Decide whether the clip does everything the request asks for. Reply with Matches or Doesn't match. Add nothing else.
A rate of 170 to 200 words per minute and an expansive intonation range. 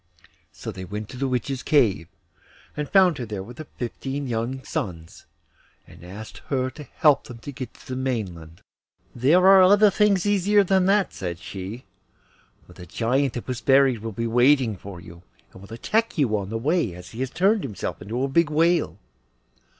Matches